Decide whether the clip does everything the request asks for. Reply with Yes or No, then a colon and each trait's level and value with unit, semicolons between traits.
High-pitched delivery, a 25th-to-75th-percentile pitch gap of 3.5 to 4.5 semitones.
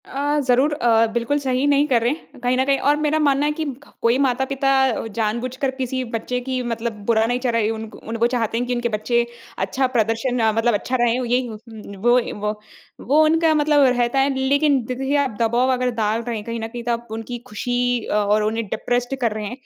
No: high, 245 Hz; average, 2.7 semitones